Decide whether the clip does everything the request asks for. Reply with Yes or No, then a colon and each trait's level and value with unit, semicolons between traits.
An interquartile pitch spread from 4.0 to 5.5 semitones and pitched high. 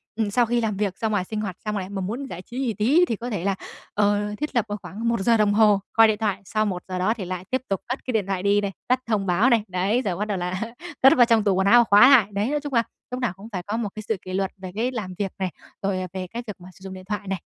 No: average, 3.2 semitones; high, 205 Hz